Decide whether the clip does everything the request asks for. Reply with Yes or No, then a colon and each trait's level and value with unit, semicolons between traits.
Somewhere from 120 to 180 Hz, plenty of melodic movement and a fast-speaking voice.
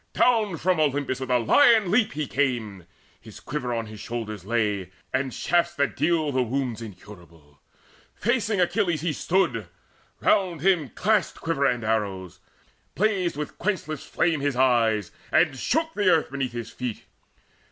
No: low, 135 Hz; wide, 7.6 semitones; average, 150 wpm